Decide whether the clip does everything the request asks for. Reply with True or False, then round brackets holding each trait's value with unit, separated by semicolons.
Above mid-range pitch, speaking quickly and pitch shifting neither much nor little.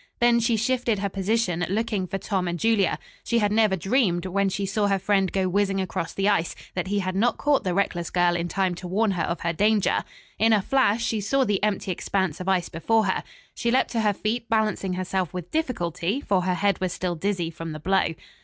True (195 Hz; 230 wpm; 3.2 semitones)